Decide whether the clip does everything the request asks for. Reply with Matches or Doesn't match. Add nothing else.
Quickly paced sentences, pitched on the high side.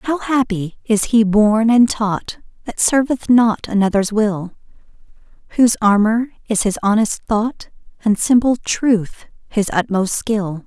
Doesn't match